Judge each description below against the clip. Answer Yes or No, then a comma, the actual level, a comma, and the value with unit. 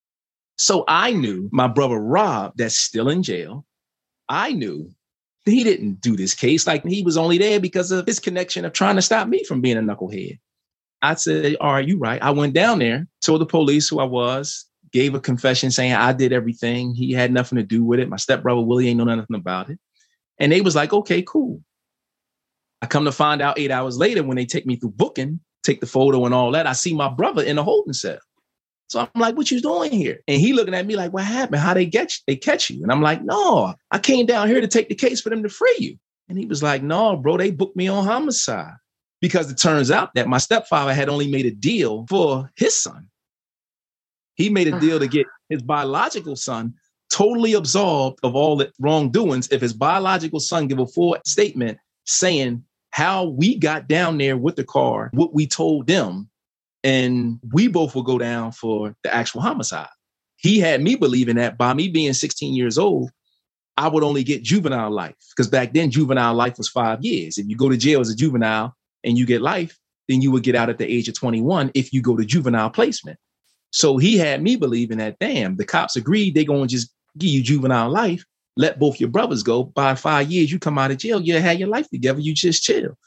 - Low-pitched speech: No, medium, 145 Hz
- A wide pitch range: Yes, wide, 6.3 semitones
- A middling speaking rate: No, fast, 225 wpm